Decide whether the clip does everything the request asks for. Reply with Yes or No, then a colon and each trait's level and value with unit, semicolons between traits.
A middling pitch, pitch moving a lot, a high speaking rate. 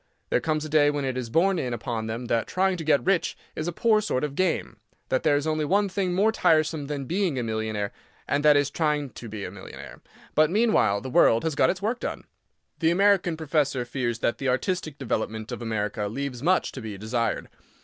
Yes: medium, 145 Hz; wide, 6.3 semitones; fast, 220 wpm